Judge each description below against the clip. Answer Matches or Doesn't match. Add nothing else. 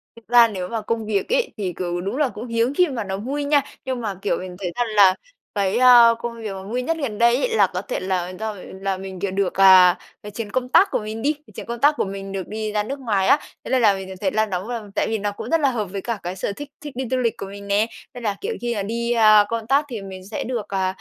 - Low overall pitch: Doesn't match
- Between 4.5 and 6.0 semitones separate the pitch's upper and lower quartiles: Doesn't match